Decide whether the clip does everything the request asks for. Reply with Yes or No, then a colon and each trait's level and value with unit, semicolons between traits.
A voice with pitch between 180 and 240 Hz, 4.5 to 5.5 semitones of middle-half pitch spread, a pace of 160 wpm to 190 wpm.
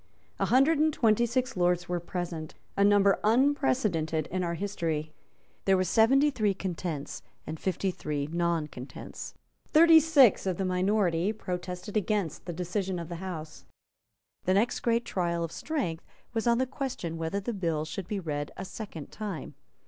Yes: medium, 185 Hz; average, 4.8 semitones; average, 165 wpm